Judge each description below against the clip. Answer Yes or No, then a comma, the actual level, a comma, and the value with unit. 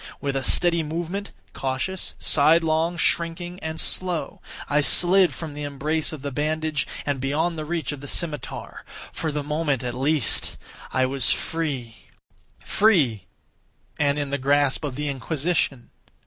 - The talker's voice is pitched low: No, medium, 150 Hz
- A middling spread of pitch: Yes, average, 3.1 semitones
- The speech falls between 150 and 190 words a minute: No, slow, 135 wpm